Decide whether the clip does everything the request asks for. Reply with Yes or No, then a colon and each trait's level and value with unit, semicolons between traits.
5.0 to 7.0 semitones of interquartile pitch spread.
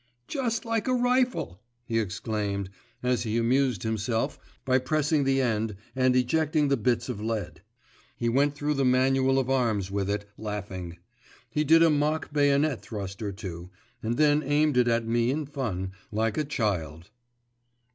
Yes: wide, 5.6 semitones